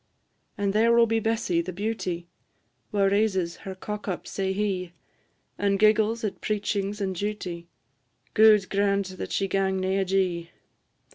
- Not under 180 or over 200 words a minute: No, average, 145 wpm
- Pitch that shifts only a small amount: Yes, narrow, 2.0 semitones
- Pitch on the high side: Yes, high, 195 Hz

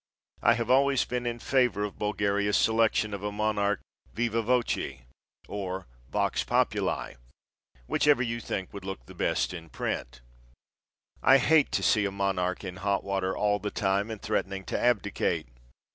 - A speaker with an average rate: Yes, average, 160 wpm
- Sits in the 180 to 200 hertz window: No, low, 105 Hz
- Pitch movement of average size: Yes, average, 3.2 semitones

